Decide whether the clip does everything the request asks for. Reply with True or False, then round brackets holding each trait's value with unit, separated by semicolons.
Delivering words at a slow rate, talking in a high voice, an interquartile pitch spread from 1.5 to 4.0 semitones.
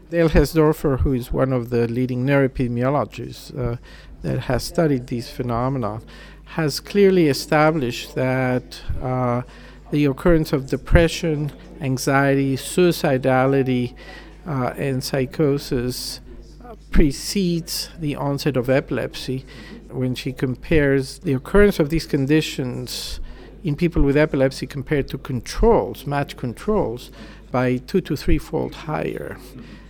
False (115 wpm; 140 Hz; 3.5 semitones)